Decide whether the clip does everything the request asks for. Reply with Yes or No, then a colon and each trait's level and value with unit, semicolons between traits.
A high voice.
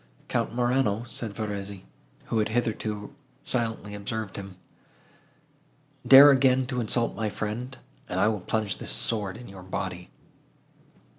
No: low, 110 Hz